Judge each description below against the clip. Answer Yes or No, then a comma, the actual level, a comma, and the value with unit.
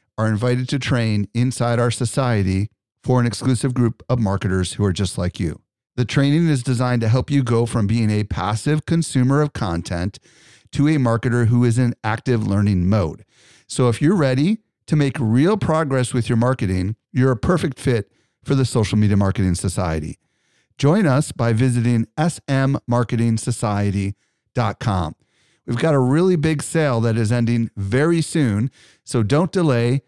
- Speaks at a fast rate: No, average, 165 wpm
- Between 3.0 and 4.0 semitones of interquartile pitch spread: No, average, 4.4 semitones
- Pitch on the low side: Yes, low, 120 Hz